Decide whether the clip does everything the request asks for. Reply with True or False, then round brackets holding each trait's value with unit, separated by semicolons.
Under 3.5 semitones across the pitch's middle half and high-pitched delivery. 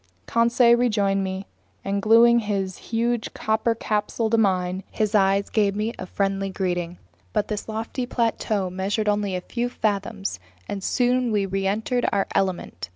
True (2.8 semitones; 205 Hz)